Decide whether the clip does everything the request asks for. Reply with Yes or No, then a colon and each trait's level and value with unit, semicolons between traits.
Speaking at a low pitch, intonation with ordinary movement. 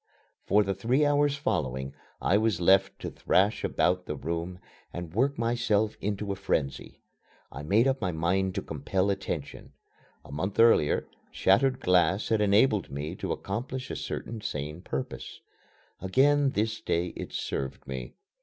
Yes: very low, 95 Hz; average, 4.8 semitones